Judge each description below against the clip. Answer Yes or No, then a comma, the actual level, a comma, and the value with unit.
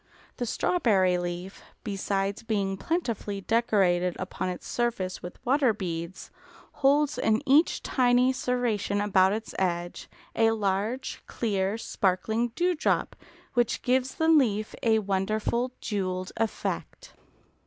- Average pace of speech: No, slow, 115 wpm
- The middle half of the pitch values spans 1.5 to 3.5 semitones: No, average, 4.3 semitones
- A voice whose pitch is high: Yes, high, 215 Hz